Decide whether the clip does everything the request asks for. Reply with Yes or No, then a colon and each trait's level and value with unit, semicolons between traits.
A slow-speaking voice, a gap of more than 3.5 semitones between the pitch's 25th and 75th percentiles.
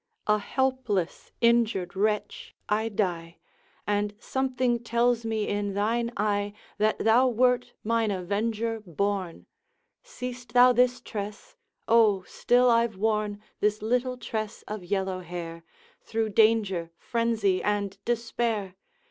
No: slow, 120 wpm; average, 2.7 semitones